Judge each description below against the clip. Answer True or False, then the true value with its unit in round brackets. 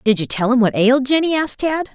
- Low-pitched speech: False (255 Hz)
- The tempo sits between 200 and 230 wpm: False (275 wpm)